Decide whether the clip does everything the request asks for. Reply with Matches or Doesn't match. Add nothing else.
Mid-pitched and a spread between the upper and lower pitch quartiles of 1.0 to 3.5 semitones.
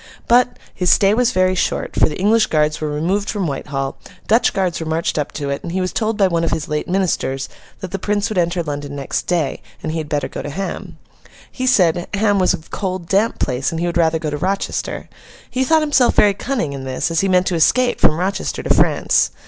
Doesn't match